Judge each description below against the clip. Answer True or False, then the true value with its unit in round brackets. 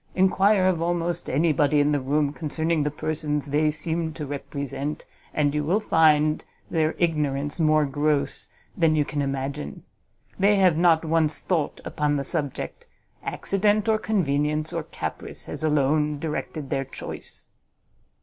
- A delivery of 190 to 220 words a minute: False (150 wpm)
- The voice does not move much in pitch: True (2.3 semitones)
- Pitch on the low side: False (150 Hz)